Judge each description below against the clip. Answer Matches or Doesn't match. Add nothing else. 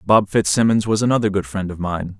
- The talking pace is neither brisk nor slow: Doesn't match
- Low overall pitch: Matches